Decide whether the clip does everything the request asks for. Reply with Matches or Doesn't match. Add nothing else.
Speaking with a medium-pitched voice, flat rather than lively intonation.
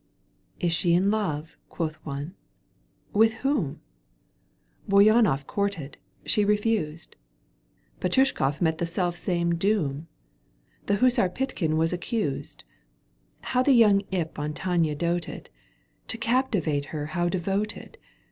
Doesn't match